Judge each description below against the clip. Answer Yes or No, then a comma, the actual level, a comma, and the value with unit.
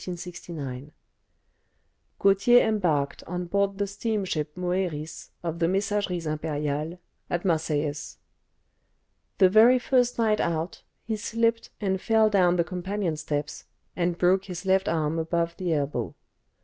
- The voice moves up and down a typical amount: Yes, average, 3.9 semitones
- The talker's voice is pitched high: No, medium, 180 Hz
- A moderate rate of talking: No, slow, 125 wpm